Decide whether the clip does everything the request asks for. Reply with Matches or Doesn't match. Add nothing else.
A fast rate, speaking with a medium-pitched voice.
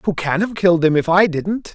Matches